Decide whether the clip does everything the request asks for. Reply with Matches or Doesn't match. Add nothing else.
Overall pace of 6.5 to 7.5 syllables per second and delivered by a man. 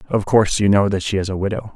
Matches